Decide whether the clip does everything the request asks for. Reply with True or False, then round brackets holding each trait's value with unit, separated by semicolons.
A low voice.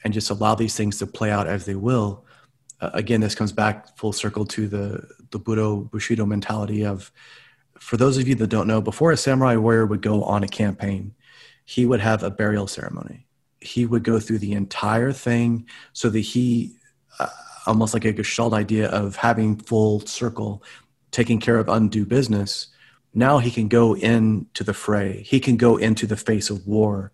True (110 Hz)